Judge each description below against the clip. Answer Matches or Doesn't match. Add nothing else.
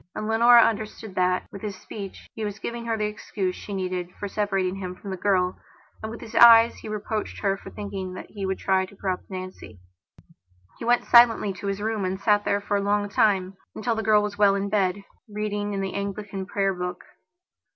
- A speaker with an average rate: Doesn't match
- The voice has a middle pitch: Doesn't match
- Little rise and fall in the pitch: Matches